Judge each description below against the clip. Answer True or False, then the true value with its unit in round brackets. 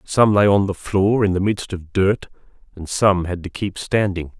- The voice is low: True (95 Hz)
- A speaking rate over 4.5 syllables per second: False (4.4 syllables/s)